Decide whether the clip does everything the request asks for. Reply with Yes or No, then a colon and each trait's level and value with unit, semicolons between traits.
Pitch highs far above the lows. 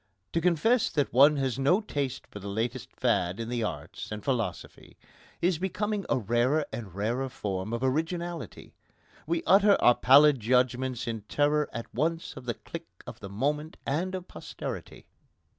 Yes: wide, 5.8 semitones